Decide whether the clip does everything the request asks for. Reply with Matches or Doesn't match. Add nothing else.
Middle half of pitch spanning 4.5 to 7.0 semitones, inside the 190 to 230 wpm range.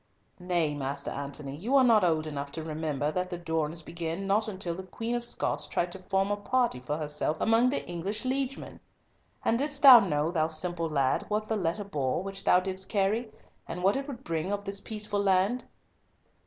Matches